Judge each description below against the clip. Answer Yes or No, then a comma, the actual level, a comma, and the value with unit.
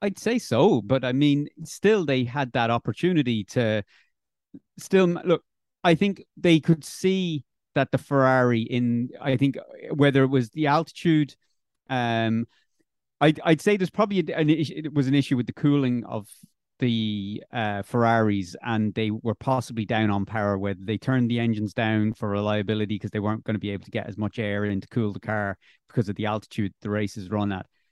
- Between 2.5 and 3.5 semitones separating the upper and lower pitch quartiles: No, wide, 5.4 semitones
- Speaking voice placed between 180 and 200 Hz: No, low, 120 Hz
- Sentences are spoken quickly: No, average, 195 wpm